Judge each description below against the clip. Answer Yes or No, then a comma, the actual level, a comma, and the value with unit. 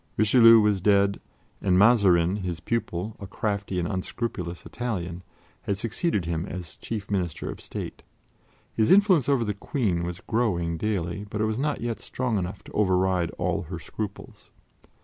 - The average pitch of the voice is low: Yes, low, 100 Hz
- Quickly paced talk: No, average, 160 wpm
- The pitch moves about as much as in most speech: Yes, average, 4.0 semitones